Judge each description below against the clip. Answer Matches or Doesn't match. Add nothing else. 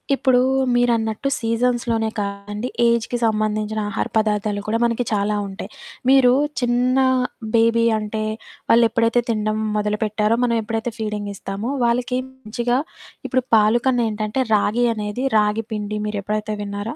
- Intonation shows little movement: Matches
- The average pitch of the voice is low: Doesn't match